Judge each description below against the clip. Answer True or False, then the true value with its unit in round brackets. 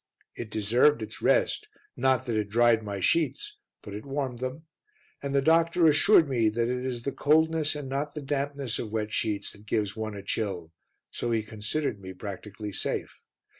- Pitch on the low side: True (120 Hz)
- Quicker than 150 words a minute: True (185 wpm)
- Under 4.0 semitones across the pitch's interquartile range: False (5.0 semitones)